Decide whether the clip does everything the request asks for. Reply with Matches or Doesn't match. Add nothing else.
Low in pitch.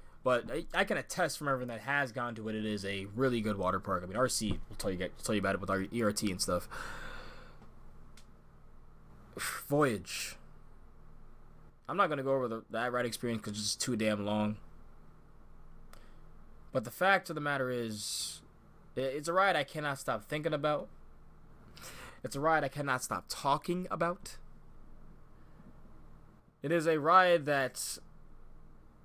Matches